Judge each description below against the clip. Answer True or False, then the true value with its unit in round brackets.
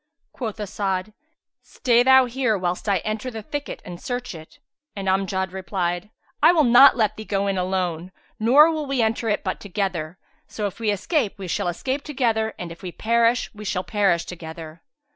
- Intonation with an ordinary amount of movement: True (4.6 semitones)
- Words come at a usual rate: True (185 wpm)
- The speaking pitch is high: True (210 Hz)